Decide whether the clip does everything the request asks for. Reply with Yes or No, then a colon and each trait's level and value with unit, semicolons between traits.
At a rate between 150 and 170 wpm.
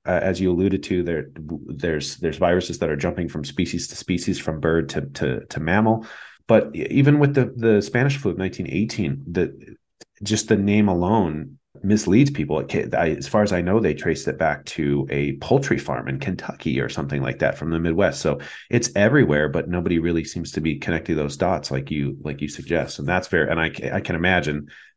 No: fast, 205 wpm